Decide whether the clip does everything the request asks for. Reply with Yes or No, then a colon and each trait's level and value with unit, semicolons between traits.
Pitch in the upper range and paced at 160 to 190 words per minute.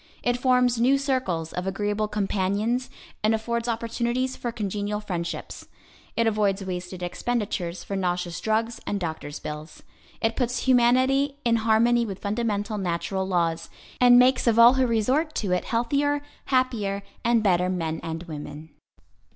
No: high, 215 Hz; average, 145 wpm